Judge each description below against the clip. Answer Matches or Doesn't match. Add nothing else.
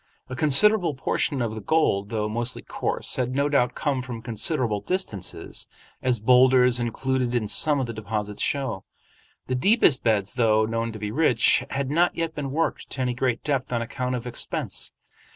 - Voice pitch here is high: Doesn't match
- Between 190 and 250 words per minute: Doesn't match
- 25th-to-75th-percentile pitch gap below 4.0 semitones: Matches